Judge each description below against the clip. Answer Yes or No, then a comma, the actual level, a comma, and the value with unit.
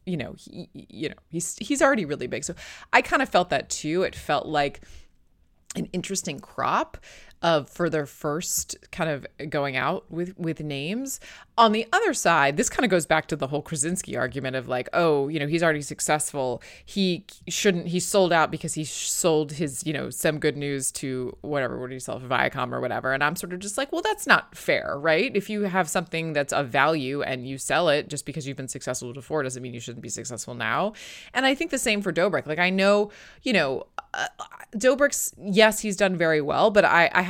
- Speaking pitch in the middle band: Yes, medium, 160 Hz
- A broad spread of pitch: Yes, wide, 6.1 semitones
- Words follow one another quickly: Yes, fast, 220 wpm